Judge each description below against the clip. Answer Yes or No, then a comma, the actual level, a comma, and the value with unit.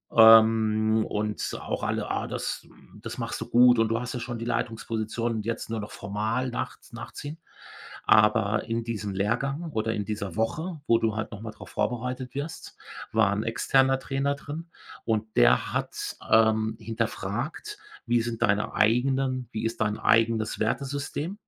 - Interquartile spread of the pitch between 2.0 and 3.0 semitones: Yes, average, 2.7 semitones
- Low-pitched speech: Yes, low, 115 Hz